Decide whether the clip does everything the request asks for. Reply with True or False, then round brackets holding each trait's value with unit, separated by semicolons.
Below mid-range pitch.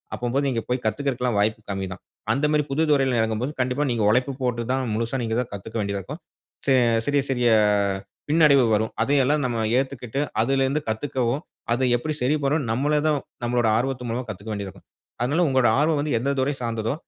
True (125 Hz)